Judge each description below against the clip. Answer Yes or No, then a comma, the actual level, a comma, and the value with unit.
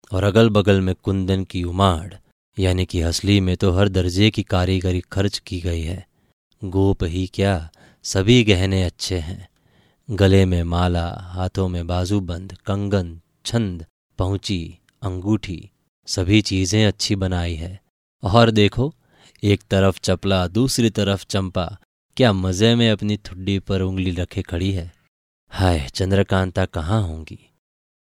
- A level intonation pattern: Yes, narrow, 2.0 semitones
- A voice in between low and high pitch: No, very low, 95 Hz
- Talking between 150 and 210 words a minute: No, average, 135 wpm